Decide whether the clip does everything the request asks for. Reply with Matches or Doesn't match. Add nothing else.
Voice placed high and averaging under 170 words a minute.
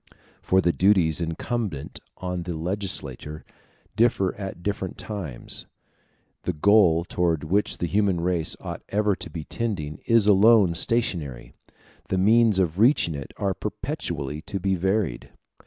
Doesn't match